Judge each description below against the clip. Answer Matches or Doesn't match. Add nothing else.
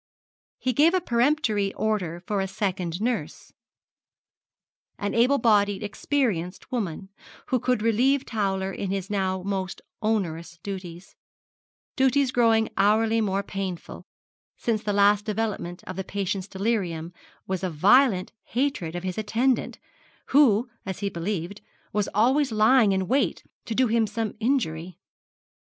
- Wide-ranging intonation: Doesn't match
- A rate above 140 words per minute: Doesn't match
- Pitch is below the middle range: Doesn't match